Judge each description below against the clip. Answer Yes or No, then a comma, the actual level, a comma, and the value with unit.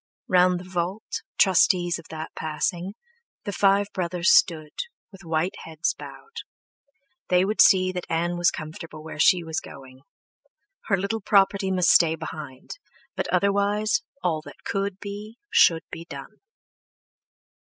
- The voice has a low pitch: No, medium, 180 Hz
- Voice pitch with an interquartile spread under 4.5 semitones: Yes, average, 3.4 semitones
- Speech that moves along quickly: No, average, 140 wpm